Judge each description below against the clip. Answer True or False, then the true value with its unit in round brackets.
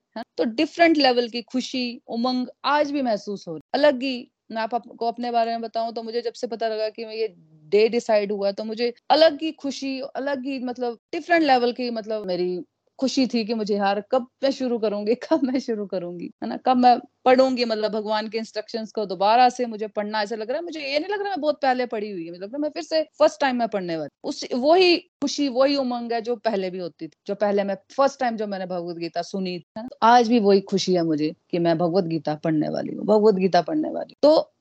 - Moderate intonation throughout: True (4.5 semitones)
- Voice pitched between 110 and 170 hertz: False (235 Hz)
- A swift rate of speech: True (230 wpm)